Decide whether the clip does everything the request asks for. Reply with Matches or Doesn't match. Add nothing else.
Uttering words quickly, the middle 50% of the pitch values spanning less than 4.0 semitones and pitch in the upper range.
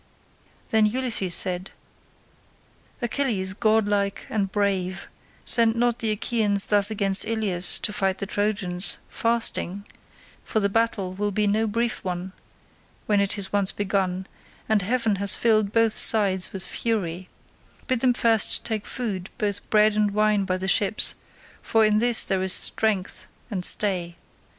Doesn't match